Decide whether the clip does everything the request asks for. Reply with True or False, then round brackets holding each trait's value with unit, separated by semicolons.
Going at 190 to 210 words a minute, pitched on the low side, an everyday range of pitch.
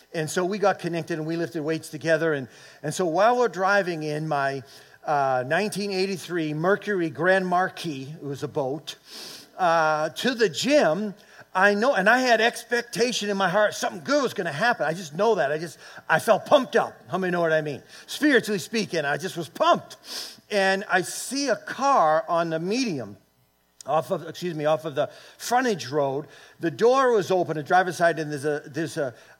False (200 wpm; 175 Hz; 5.0 semitones)